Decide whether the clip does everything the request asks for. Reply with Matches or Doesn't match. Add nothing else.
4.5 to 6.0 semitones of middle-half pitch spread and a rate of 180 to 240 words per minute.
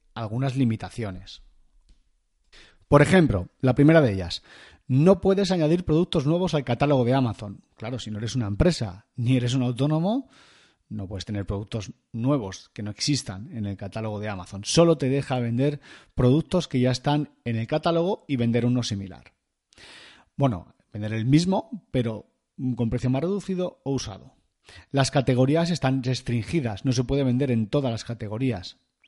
Doesn't match